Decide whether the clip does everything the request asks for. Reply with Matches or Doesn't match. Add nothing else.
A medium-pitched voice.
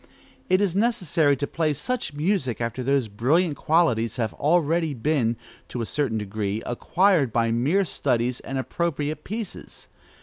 Matches